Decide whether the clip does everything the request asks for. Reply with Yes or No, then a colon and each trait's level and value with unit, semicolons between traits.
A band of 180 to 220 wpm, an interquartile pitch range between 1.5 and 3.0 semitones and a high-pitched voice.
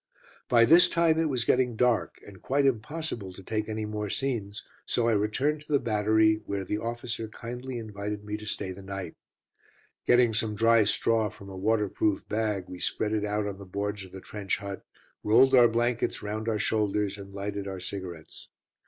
No: average, 190 wpm; average, 2.7 semitones; low, 105 Hz